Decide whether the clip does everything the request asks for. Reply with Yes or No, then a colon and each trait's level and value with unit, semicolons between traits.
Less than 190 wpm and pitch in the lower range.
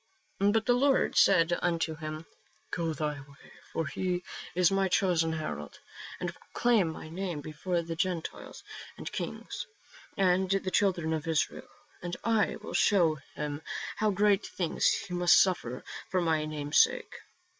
No: average, 155 wpm; medium, 175 Hz